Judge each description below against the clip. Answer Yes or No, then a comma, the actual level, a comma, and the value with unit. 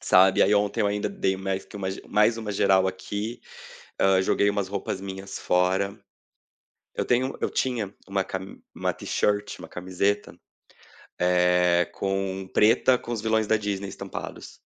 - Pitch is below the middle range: Yes, low, 100 Hz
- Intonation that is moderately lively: No, narrow, 1.7 semitones